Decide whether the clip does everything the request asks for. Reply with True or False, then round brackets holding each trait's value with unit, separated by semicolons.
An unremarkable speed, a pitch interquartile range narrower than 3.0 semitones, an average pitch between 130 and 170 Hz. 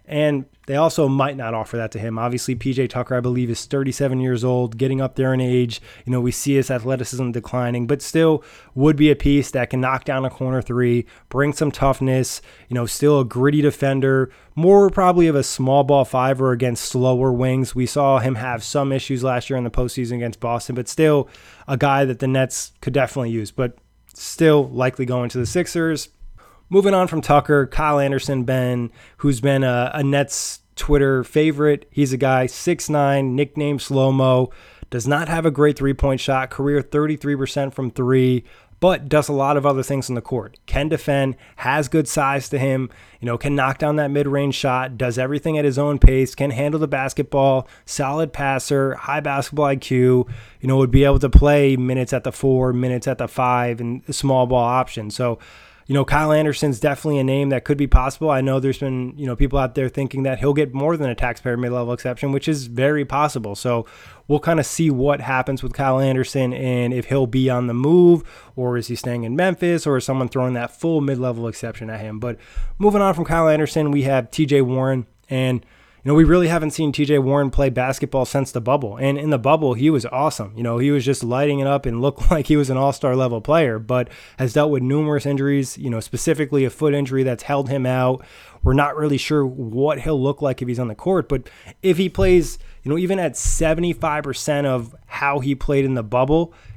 False (215 wpm; 2.4 semitones; 135 Hz)